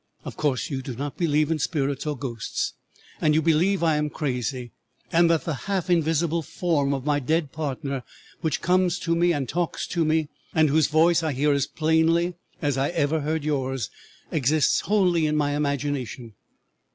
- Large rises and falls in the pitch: No, average, 2.9 semitones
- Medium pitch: Yes, medium, 150 Hz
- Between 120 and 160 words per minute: No, average, 180 wpm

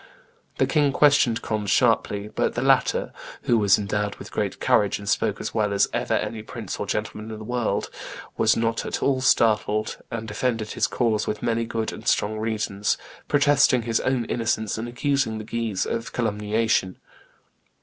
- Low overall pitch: Yes, low, 110 Hz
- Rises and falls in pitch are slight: Yes, narrow, 2.0 semitones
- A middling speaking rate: Yes, average, 175 wpm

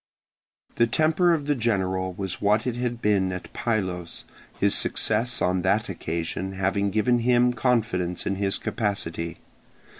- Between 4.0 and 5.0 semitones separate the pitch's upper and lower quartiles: Yes, average, 4.4 semitones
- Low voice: Yes, low, 100 Hz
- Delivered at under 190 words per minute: Yes, average, 145 wpm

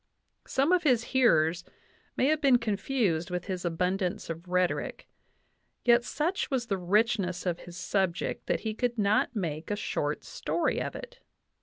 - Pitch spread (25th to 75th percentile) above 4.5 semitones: Yes, wide, 5.6 semitones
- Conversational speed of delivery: Yes, average, 160 wpm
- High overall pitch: Yes, high, 200 Hz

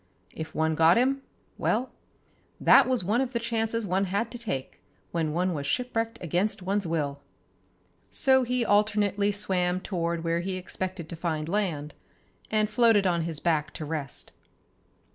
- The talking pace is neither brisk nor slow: Yes, average, 160 wpm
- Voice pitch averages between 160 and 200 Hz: Yes, medium, 185 Hz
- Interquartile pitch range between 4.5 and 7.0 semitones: Yes, average, 5.2 semitones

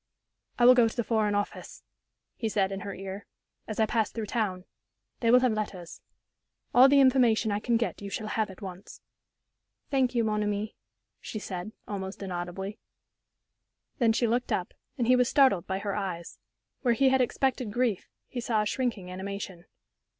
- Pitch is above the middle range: Yes, high, 215 Hz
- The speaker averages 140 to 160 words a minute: No, average, 180 wpm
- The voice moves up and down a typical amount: Yes, average, 3.7 semitones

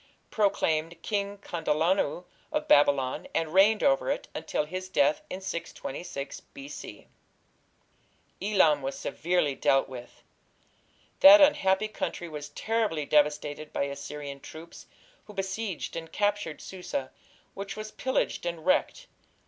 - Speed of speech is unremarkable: No, slow, 120 wpm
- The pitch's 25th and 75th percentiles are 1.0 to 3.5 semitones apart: No, wide, 5.6 semitones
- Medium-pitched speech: Yes, medium, 175 Hz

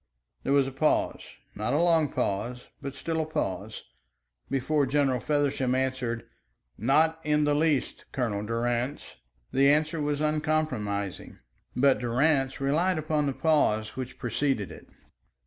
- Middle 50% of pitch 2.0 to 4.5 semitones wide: Yes, average, 3.7 semitones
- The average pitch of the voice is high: No, low, 135 Hz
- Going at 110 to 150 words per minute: Yes, slow, 135 wpm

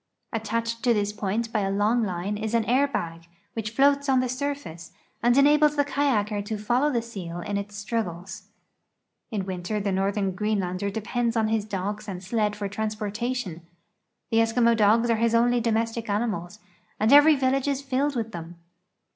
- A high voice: Yes, high, 220 Hz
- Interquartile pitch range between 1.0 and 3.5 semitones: Yes, average, 3.1 semitones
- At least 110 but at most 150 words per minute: No, average, 175 wpm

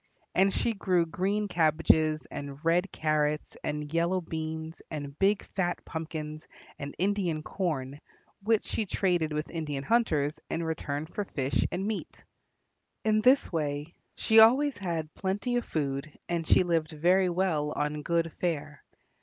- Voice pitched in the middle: Yes, medium, 165 Hz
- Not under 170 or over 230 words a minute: No, average, 145 wpm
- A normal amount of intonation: Yes, average, 3.9 semitones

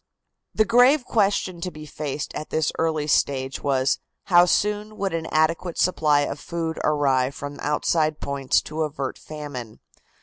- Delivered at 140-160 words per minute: Yes, average, 155 wpm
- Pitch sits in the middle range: Yes, medium, 155 Hz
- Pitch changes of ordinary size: Yes, average, 3.5 semitones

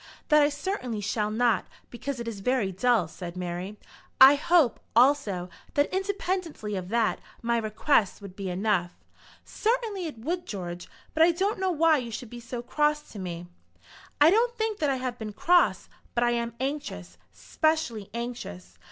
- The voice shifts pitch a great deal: Yes, wide, 7.1 semitones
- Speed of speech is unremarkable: Yes, average, 170 wpm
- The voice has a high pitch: Yes, high, 240 Hz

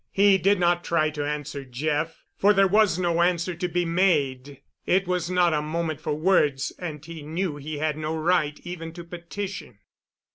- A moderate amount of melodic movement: Yes, average, 3.0 semitones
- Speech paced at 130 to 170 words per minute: No, average, 185 wpm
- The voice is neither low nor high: Yes, medium, 165 Hz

